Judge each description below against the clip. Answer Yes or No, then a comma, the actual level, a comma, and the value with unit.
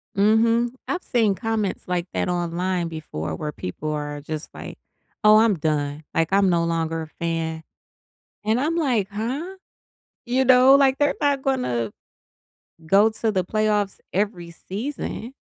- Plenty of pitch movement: Yes, wide, 6.3 semitones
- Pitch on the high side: Yes, high, 200 Hz